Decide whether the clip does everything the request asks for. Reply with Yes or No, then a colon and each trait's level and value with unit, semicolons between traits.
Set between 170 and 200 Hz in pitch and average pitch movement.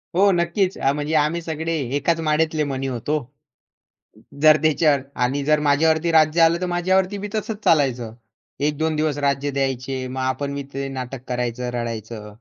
No: medium, 150 Hz; average, 3.7 semitones